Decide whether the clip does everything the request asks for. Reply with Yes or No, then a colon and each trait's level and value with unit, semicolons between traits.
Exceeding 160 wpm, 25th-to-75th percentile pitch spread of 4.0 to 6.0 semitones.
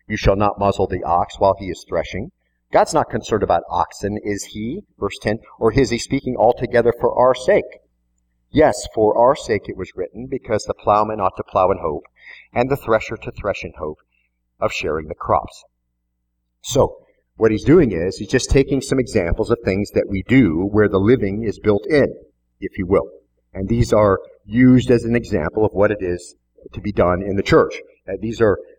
Yes: average, 200 wpm; average, 4.3 semitones